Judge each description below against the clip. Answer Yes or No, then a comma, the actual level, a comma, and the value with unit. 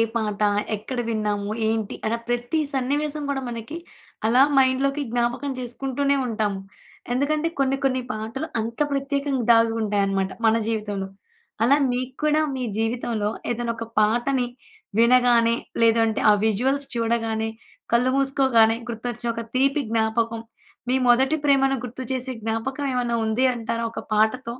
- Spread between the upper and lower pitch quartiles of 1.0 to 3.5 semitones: Yes, average, 3.1 semitones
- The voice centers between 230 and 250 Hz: Yes, high, 240 Hz